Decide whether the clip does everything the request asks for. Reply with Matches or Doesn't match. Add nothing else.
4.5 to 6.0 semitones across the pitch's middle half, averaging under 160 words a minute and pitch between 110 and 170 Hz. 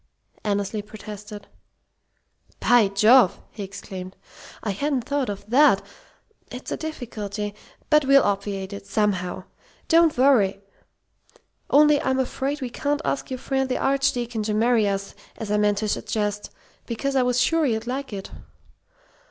Doesn't match